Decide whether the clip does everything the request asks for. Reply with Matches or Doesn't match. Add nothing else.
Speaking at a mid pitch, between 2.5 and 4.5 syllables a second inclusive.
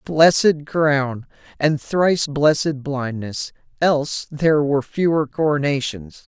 Matches